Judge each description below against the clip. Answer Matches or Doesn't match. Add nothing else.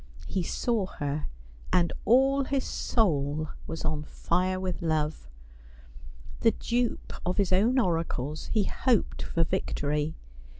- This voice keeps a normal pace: Doesn't match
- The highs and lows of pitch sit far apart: Matches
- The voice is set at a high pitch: Doesn't match